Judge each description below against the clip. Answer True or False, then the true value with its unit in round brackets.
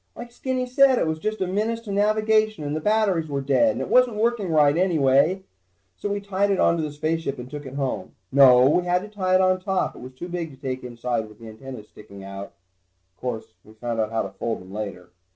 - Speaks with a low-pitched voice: False (160 Hz)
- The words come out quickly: True (240 wpm)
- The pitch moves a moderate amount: False (8.3 semitones)